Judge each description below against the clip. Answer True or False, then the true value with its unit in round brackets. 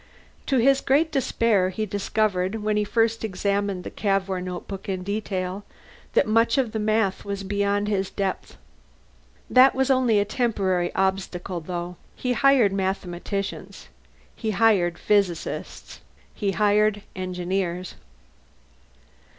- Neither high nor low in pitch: False (200 Hz)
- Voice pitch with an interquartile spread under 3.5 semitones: True (2.8 semitones)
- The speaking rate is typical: False (125 wpm)